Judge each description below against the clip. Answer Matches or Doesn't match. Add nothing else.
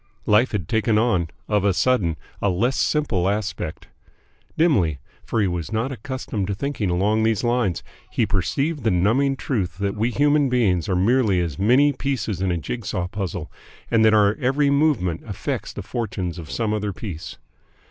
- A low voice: Matches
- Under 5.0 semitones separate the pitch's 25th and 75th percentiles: Doesn't match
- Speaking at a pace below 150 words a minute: Doesn't match